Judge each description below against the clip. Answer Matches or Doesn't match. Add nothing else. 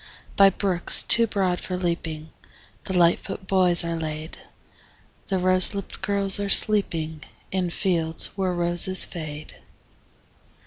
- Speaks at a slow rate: Matches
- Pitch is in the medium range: Matches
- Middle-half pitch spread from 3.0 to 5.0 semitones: Doesn't match